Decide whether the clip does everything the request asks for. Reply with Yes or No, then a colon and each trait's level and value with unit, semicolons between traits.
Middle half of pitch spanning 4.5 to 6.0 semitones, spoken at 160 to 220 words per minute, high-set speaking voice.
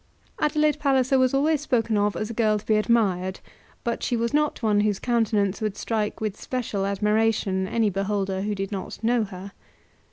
No: average, 3.2 semitones; average, 185 wpm; high, 215 Hz